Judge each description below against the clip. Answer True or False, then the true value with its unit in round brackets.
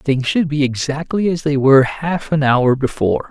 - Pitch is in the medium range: True (145 Hz)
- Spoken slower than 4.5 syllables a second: False (4.9 syllables/s)